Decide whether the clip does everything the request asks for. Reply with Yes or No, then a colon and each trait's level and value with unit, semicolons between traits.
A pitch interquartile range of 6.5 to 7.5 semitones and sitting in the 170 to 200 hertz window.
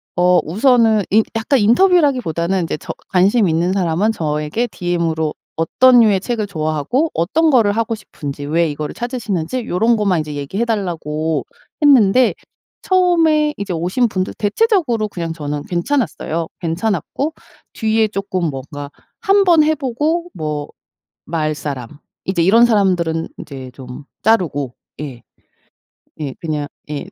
Yes: wide, 7.0 semitones; high, 190 Hz